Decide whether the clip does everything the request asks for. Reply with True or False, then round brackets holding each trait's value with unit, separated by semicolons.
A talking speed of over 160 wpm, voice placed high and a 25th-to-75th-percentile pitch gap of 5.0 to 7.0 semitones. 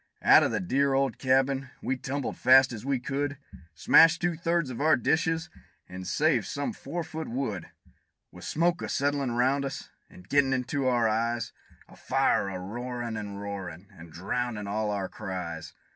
False (175 wpm; 125 Hz; 5.3 semitones)